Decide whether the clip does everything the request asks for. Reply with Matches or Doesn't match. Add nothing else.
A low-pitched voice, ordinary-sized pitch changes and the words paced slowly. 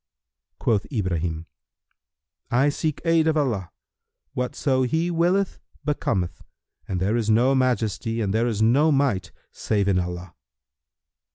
Doesn't match